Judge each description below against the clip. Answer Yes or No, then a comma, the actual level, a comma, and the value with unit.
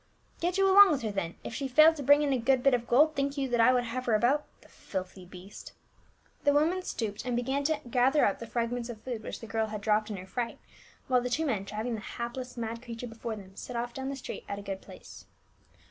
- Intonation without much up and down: No, average, 3.8 semitones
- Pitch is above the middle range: Yes, high, 240 Hz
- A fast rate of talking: Yes, fast, 265 wpm